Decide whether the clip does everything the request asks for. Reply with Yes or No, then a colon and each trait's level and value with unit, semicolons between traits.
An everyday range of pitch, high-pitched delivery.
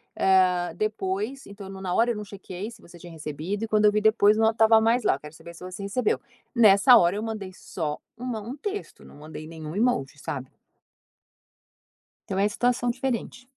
Yes: average, 4.2 semitones; high, 205 Hz